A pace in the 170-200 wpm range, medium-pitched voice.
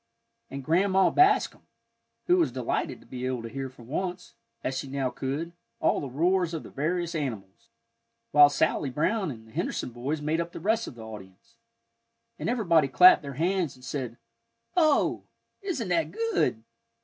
Yes: average, 175 wpm; medium, 150 Hz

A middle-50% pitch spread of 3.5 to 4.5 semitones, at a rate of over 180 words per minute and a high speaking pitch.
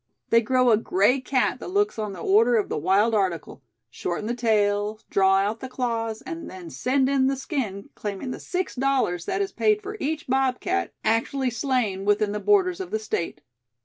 No: average, 5.0 semitones; average, 195 wpm; high, 230 Hz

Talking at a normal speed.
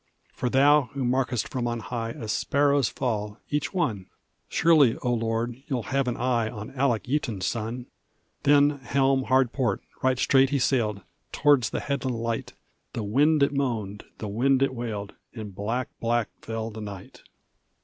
Yes: average, 165 wpm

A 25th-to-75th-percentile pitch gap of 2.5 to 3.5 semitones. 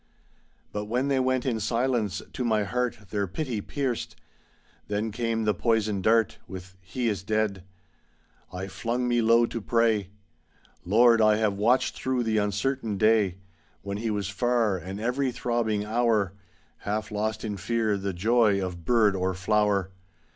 Yes: average, 2.9 semitones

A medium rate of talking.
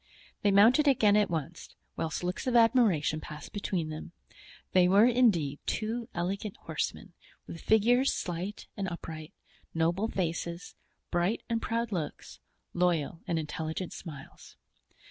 No: slow, 130 wpm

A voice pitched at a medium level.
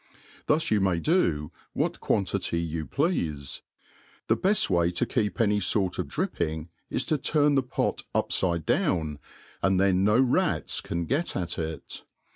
No: very low, 95 Hz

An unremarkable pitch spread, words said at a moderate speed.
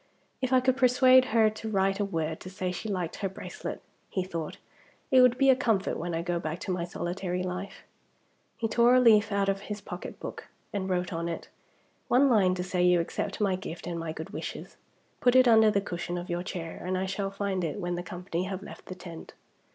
No: average, 3.6 semitones; fast, 230 wpm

